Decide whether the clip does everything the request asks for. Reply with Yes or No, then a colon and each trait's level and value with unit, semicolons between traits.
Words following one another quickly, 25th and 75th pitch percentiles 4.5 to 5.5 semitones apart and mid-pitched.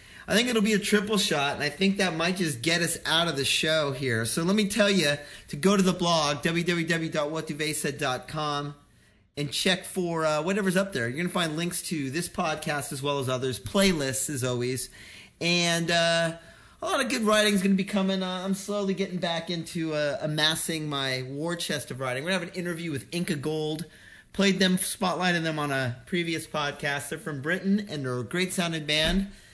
No: fast, 210 wpm; average, 4.1 semitones; medium, 165 Hz